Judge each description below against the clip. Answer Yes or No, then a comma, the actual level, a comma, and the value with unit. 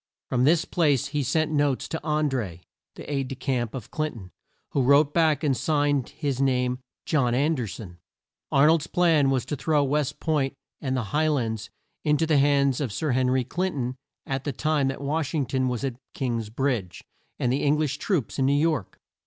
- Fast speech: Yes, fast, 210 wpm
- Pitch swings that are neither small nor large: Yes, average, 3.1 semitones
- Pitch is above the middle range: No, medium, 140 Hz